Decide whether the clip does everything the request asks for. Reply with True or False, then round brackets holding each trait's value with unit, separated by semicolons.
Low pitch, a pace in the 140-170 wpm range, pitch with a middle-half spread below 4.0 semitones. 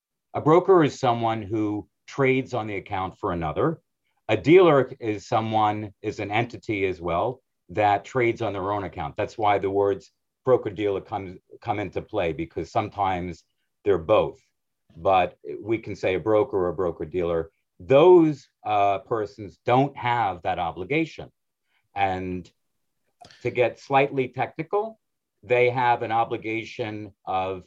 False (110 Hz; 145 wpm; 4.4 semitones)